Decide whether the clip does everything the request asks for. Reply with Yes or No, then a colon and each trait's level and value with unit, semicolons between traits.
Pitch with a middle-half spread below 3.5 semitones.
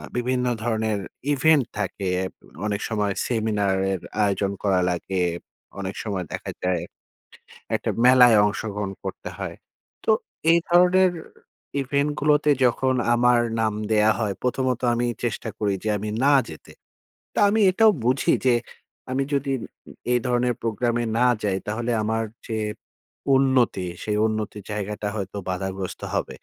No: average, 3.9 semitones